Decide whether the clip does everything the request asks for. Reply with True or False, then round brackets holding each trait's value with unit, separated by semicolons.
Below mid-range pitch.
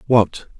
True (115 Hz)